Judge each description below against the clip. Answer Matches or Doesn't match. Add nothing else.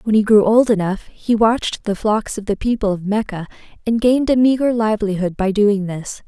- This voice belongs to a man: Doesn't match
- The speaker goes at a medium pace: Doesn't match